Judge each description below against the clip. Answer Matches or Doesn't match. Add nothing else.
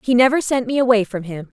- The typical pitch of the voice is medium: Doesn't match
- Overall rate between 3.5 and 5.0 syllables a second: Doesn't match